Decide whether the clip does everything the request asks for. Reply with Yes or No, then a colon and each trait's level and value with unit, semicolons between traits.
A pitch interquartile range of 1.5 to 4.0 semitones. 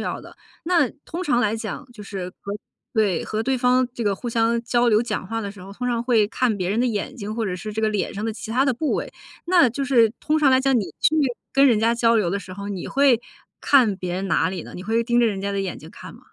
Yes: average, 3.7 semitones